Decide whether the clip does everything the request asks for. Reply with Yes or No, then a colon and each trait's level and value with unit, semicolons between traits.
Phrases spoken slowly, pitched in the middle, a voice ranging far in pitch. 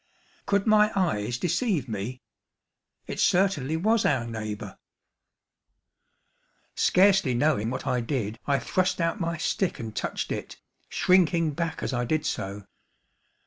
Yes: slow, 130 wpm; medium, 155 Hz; wide, 7.5 semitones